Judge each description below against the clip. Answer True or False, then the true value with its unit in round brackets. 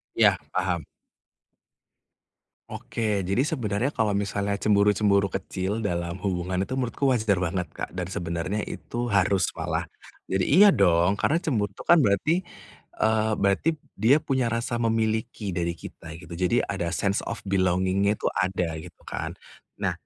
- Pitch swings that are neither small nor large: True (3.5 semitones)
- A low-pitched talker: True (100 Hz)